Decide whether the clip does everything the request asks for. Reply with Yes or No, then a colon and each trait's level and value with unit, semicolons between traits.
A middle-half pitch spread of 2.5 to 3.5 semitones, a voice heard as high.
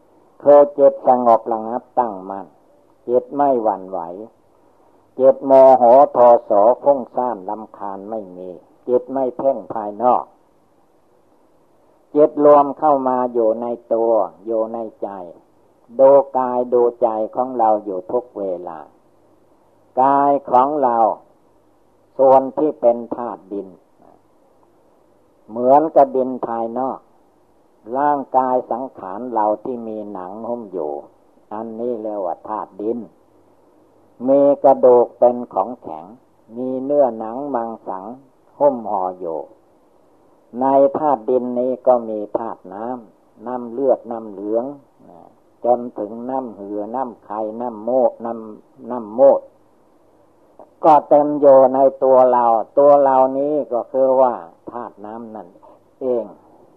No: average, 3.2 semitones; low, 125 Hz